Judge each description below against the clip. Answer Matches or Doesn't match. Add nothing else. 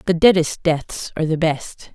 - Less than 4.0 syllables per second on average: Doesn't match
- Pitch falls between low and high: Matches